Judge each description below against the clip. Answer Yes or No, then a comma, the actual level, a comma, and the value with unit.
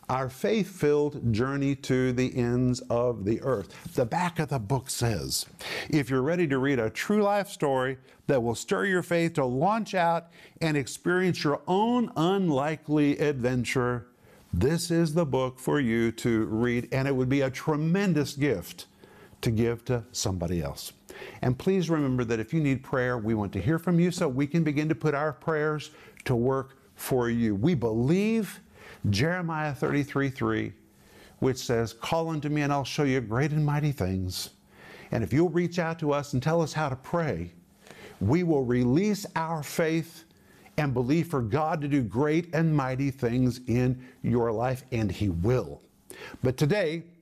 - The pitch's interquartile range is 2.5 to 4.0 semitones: No, average, 4.7 semitones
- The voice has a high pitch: No, medium, 140 Hz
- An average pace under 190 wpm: Yes, average, 175 wpm